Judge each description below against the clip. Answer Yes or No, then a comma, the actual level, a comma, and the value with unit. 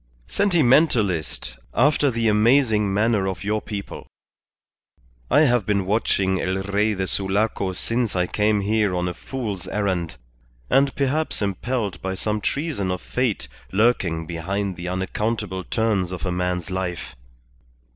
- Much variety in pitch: No, average, 3.8 semitones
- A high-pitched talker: No, low, 100 Hz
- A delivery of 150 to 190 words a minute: No, slow, 135 wpm